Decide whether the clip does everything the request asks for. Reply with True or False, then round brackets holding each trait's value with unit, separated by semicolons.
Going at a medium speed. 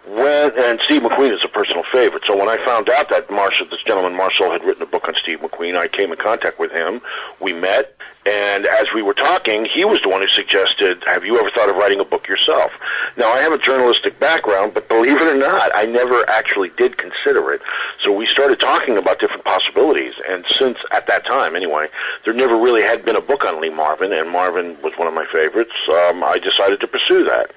False (230 wpm)